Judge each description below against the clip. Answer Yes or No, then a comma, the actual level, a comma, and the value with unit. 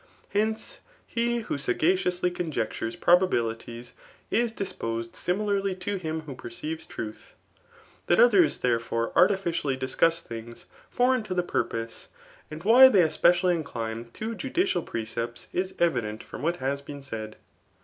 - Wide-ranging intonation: Yes, wide, 8.5 semitones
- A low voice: No, medium, 165 Hz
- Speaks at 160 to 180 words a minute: No, slow, 135 wpm